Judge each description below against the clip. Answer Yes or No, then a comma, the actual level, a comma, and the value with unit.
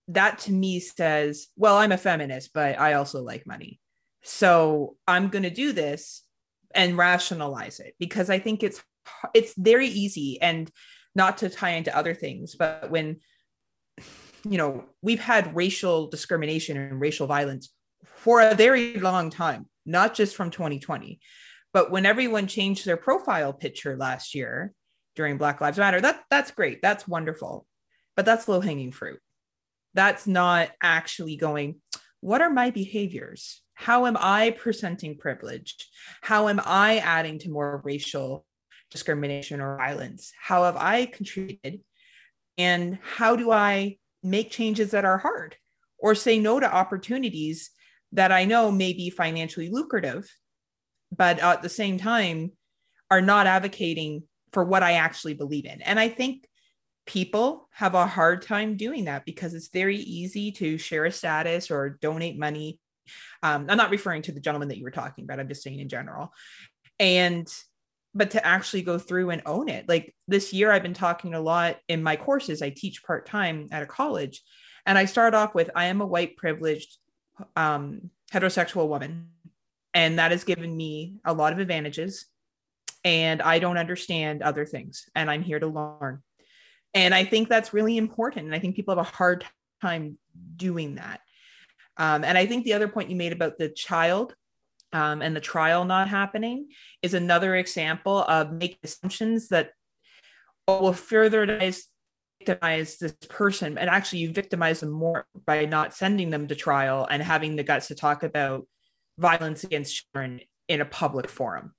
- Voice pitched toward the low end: No, medium, 175 Hz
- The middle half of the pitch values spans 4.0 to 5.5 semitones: Yes, average, 4.4 semitones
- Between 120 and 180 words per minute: Yes, average, 165 wpm